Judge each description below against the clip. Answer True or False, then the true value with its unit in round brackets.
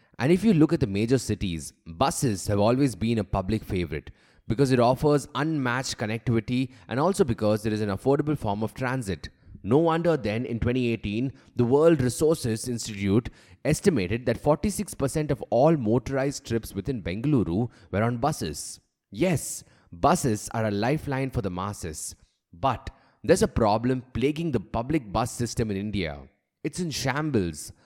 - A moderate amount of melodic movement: True (5.0 semitones)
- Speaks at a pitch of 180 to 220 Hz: False (120 Hz)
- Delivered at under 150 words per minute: False (155 wpm)